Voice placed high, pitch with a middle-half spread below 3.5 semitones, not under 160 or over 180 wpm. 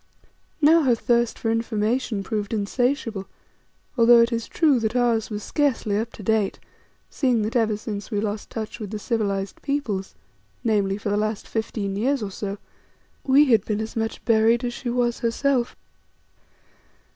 Yes: high, 225 Hz; narrow, 2.5 semitones; average, 165 wpm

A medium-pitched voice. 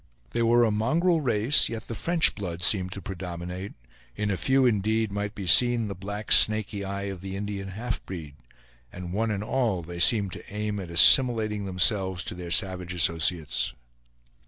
No: low, 100 Hz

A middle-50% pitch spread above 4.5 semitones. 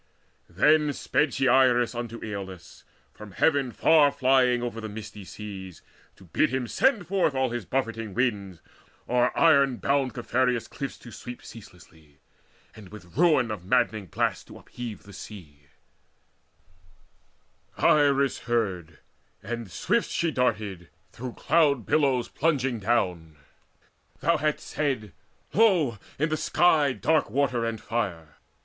Yes: average, 5.3 semitones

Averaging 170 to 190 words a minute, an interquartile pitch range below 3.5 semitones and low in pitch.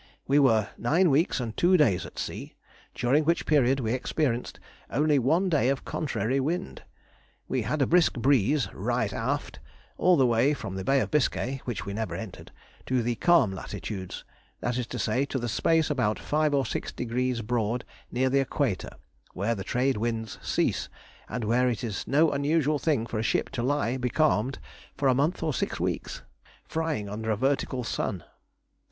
No: average, 185 wpm; average, 4.3 semitones; low, 130 Hz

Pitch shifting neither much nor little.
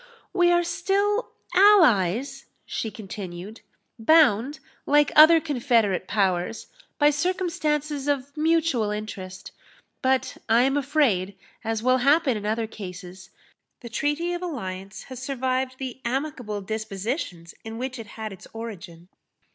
No: wide, 6.1 semitones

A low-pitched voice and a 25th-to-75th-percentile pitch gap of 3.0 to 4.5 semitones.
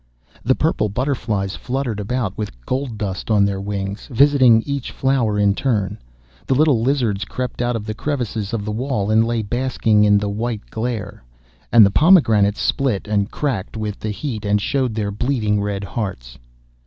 Yes: low, 110 Hz; average, 3.8 semitones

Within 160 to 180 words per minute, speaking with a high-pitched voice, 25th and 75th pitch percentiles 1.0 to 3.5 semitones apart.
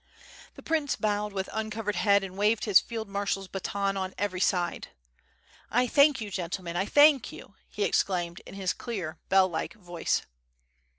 Yes: average, 165 wpm; high, 200 Hz; average, 2.7 semitones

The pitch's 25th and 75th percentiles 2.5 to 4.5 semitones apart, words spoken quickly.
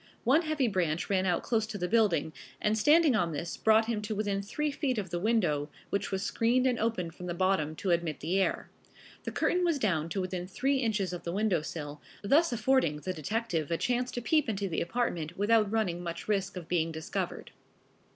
No: average, 5.2 semitones; fast, 210 wpm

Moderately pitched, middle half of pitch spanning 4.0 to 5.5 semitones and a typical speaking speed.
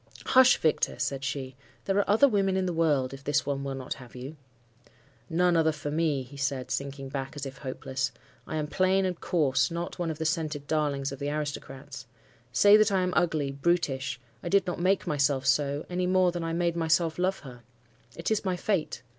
No: medium, 155 Hz; average, 4.4 semitones; fast, 210 wpm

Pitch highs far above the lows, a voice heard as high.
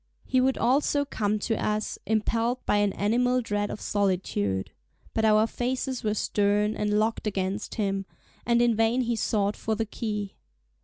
No: narrow, 2.5 semitones; high, 215 Hz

